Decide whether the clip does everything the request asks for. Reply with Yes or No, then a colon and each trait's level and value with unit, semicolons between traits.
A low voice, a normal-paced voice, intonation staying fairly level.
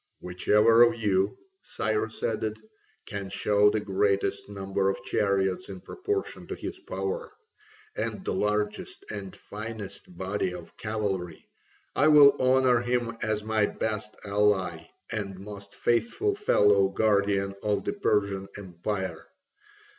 No: low, 105 Hz; slow, 125 wpm; narrow, 2.3 semitones